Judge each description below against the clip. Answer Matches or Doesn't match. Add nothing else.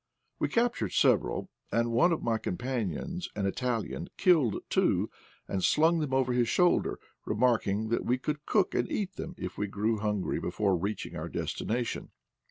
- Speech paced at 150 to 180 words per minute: Matches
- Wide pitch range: Matches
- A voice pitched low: Matches